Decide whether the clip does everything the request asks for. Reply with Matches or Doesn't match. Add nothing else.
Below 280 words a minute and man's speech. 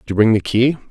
Doesn't match